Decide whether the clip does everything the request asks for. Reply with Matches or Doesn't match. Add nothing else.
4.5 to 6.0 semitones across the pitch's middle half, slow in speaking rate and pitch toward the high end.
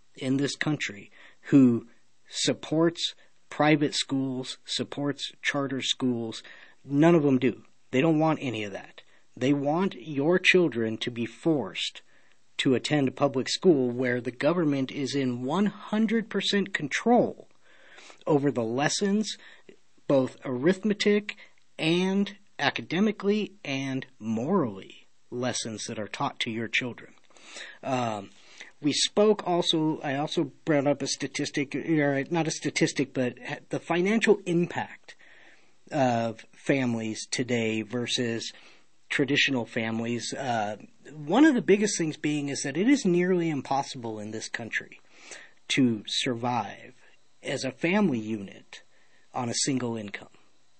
Doesn't match